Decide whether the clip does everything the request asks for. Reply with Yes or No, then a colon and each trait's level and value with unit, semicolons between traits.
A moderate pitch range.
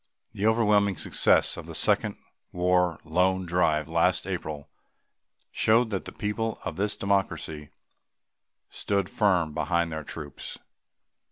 Yes: average, 4.2 semitones